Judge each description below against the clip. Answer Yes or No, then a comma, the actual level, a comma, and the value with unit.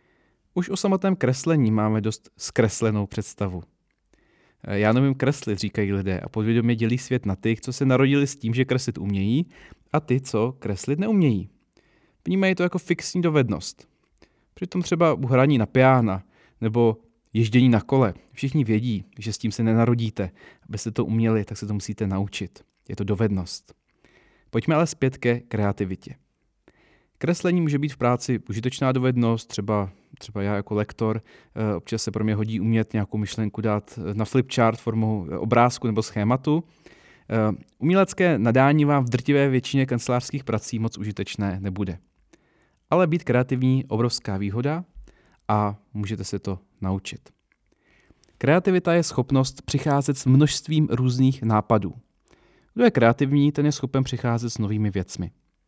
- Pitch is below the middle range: Yes, low, 115 Hz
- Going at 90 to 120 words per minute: No, average, 150 wpm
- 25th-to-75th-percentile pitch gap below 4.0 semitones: No, average, 4.3 semitones